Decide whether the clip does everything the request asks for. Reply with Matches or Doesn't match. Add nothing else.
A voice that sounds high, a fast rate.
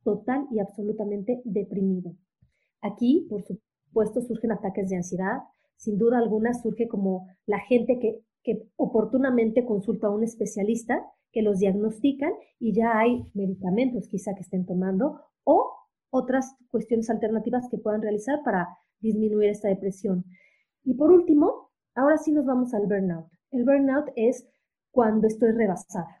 Doesn't match